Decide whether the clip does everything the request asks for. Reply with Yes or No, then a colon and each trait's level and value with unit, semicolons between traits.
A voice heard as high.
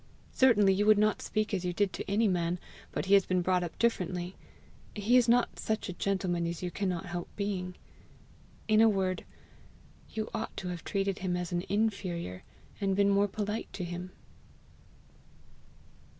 Yes: high, 195 Hz